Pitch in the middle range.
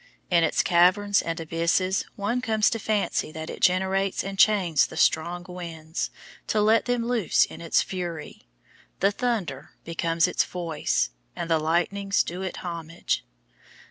Yes: medium, 180 Hz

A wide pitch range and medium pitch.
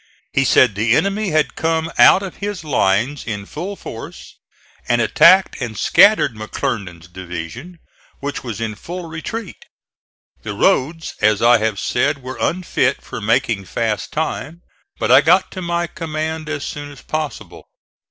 Yes: wide, 7.0 semitones; medium, 145 Hz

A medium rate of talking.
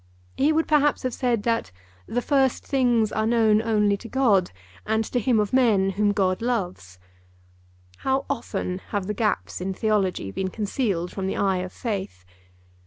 Yes: average, 170 wpm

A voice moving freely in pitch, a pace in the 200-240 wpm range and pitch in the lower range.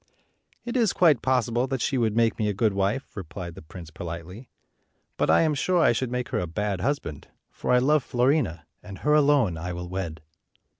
Yes: wide, 6.9 semitones; fast, 205 wpm; low, 115 Hz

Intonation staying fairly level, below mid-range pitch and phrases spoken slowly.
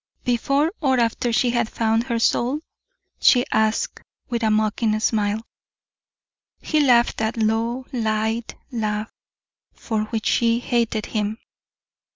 No: narrow, 1.8 semitones; high, 230 Hz; slow, 125 wpm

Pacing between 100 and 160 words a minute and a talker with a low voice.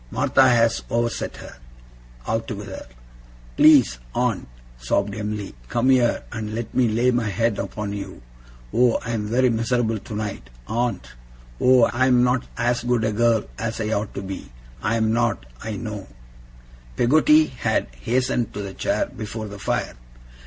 Yes: average, 155 wpm; low, 115 Hz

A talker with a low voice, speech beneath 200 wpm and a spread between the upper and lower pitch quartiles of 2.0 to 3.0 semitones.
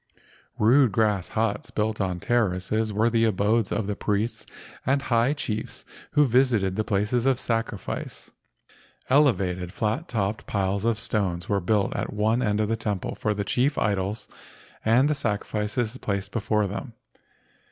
Yes: low, 110 Hz; average, 150 wpm; narrow, 2.5 semitones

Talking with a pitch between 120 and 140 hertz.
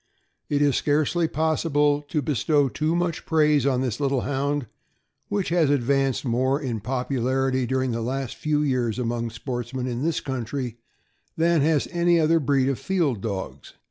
Yes: low, 135 Hz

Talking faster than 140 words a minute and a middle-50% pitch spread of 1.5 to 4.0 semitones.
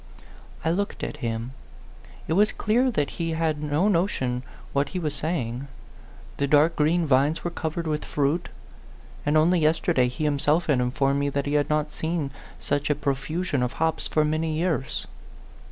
Yes: average, 170 wpm; average, 2.8 semitones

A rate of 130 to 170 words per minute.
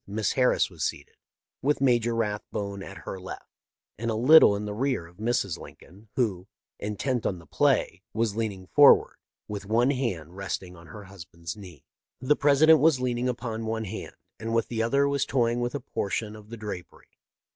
No: average, 185 wpm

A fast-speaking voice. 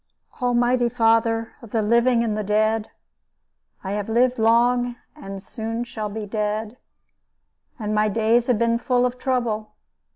No: average, 150 wpm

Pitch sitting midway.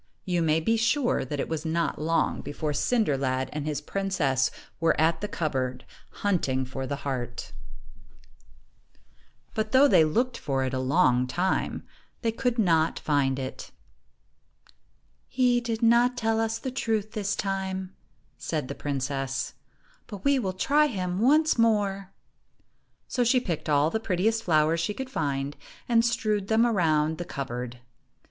Yes: medium, 180 Hz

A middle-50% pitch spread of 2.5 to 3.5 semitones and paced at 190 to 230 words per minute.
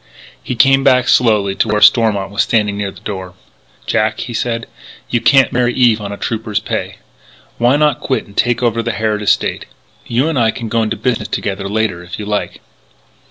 Yes: average, 2.8 semitones; average, 200 wpm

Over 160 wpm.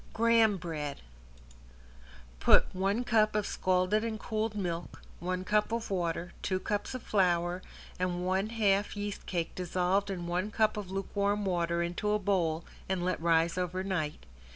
No: average, 155 wpm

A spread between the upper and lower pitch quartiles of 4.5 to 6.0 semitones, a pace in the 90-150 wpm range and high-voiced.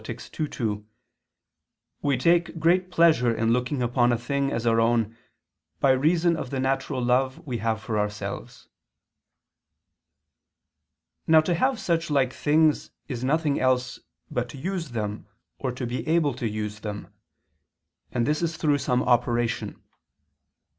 No: average, 5.0 semitones; average, 145 wpm; low, 130 Hz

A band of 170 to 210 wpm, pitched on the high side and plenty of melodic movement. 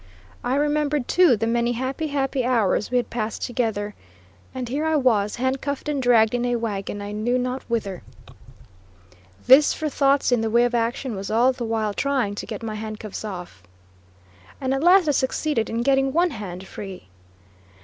No: average, 180 wpm; high, 245 Hz; average, 3.9 semitones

